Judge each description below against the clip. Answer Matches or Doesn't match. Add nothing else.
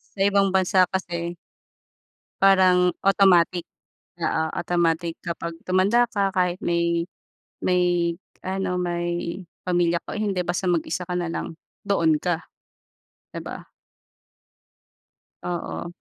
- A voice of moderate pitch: Matches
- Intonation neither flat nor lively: Doesn't match